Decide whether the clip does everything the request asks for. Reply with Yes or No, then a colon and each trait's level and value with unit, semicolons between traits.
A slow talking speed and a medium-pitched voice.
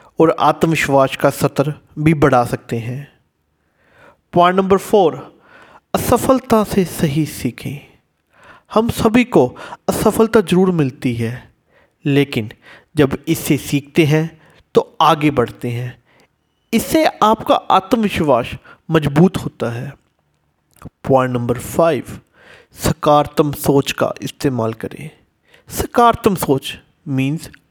Yes: slow, 105 wpm; medium, 145 Hz